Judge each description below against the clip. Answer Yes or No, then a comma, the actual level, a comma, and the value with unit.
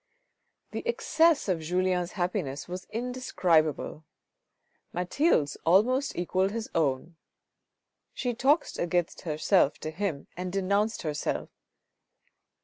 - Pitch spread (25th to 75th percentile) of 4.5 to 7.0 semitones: Yes, wide, 5.5 semitones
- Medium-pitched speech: Yes, medium, 180 Hz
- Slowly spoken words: Yes, slow, 100 wpm